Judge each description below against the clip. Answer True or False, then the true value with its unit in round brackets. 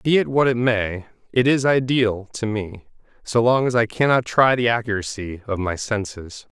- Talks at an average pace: True (190 wpm)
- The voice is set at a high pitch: False (115 Hz)